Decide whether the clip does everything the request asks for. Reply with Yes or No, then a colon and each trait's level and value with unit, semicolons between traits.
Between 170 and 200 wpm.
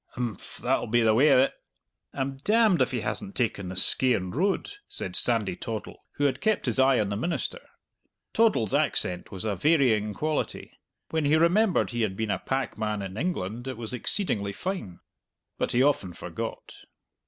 Yes: average, 175 wpm